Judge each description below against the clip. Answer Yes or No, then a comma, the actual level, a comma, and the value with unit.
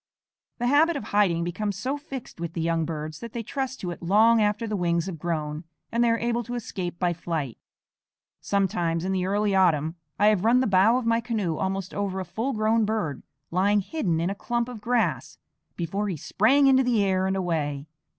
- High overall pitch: Yes, high, 195 Hz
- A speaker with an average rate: No, fast, 210 wpm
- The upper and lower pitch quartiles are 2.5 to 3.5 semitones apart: No, average, 5.1 semitones